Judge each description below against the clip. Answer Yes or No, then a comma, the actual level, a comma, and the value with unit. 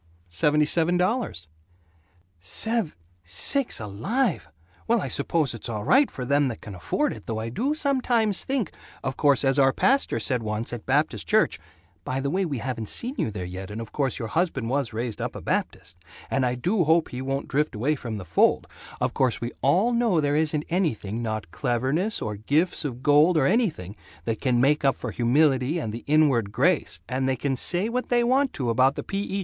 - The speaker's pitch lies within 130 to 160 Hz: Yes, low, 135 Hz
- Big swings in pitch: Yes, wide, 7.4 semitones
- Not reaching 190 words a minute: No, fast, 205 wpm